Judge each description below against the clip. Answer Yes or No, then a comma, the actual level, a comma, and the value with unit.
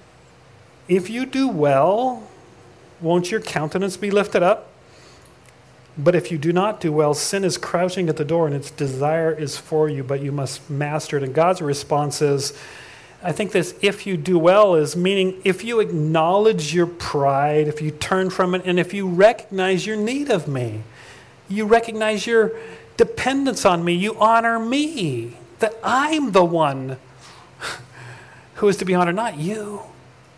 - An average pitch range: No, wide, 6.0 semitones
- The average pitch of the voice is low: No, medium, 175 Hz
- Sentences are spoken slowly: No, average, 170 wpm